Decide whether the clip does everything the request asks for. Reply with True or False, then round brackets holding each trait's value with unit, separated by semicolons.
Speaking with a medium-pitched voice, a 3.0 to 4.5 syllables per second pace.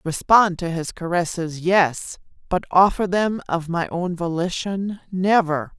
True (180 Hz; 4.1 syllables/s)